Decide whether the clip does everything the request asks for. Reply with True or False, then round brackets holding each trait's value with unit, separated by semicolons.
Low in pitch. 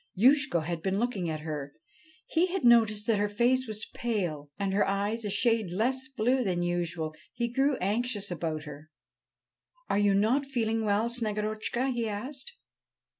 False (215 Hz)